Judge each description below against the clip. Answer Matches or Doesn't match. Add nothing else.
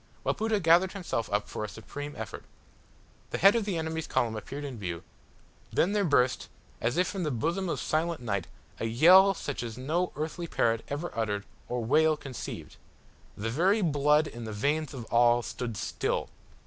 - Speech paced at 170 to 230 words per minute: Matches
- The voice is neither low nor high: Matches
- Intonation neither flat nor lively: Doesn't match